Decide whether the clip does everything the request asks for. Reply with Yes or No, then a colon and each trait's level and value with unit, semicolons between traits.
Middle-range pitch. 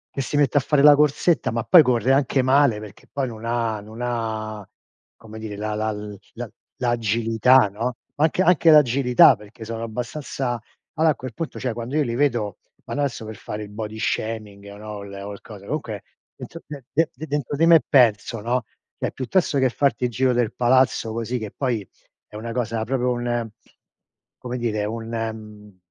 No: low, 120 Hz